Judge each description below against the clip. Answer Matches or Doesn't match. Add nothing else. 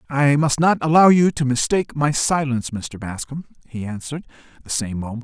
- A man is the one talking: Matches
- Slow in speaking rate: Doesn't match